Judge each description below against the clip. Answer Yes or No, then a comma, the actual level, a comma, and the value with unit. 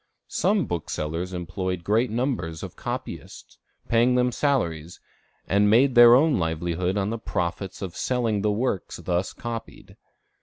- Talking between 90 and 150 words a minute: Yes, average, 140 wpm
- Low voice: Yes, low, 105 Hz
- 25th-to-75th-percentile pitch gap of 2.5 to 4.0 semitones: No, wide, 5.5 semitones